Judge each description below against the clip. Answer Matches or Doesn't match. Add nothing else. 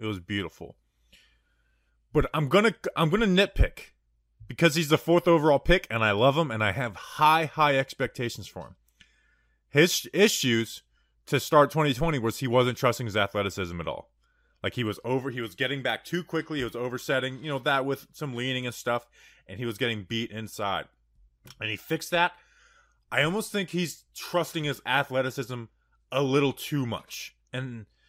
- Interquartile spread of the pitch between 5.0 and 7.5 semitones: Matches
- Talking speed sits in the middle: Matches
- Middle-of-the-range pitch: Doesn't match